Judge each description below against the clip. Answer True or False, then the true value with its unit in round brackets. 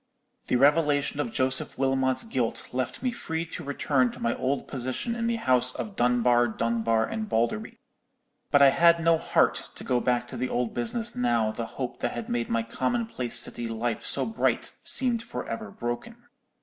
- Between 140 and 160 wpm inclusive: False (185 wpm)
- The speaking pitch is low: True (130 Hz)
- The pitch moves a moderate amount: False (5.7 semitones)